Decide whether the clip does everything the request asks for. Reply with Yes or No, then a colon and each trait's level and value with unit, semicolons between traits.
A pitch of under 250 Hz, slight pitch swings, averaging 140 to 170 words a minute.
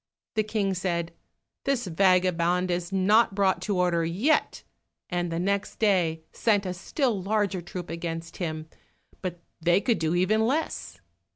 No: medium, 185 Hz; average, 3.1 semitones; average, 145 wpm